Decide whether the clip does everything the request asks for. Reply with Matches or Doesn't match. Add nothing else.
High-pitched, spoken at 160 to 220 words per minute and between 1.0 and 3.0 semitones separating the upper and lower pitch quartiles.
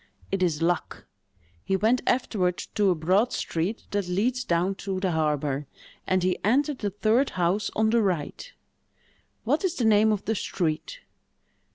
Doesn't match